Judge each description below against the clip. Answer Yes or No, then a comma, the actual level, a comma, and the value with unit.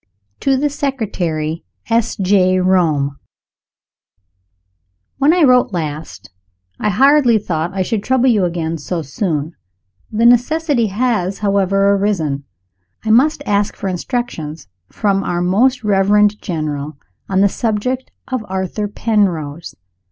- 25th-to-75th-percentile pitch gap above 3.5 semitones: Yes, wide, 5.4 semitones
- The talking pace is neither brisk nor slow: No, slow, 120 wpm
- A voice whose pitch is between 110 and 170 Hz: No, high, 200 Hz